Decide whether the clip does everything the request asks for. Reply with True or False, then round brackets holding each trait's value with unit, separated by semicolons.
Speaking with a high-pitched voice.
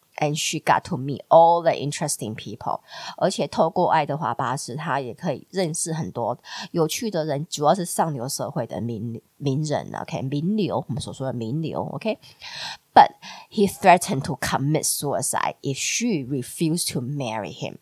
False (155 Hz)